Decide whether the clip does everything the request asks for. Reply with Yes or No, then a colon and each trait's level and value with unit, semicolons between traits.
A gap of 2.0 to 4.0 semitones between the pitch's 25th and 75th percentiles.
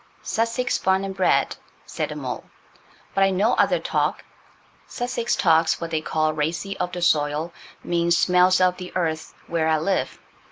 Yes: average, 3.1 semitones